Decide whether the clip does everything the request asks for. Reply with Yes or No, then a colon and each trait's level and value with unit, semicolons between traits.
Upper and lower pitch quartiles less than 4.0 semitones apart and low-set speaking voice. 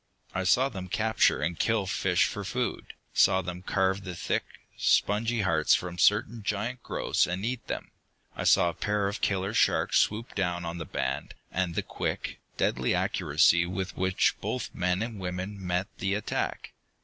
Yes: average, 2.8 semitones; very low, 95 Hz